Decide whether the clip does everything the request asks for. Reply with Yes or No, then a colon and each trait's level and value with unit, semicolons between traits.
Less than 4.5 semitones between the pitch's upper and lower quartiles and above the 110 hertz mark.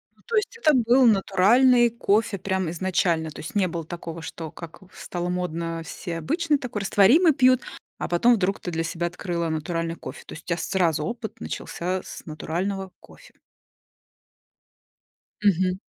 No: average, 5.3 semitones; medium, 185 Hz